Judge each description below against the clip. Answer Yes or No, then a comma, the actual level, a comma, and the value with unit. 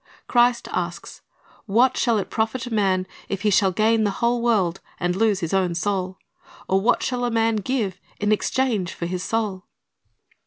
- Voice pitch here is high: Yes, high, 210 Hz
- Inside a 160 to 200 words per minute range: Yes, average, 180 wpm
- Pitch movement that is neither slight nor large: Yes, average, 3.7 semitones